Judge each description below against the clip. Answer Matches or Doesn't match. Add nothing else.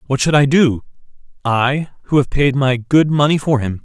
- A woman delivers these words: Doesn't match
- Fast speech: Doesn't match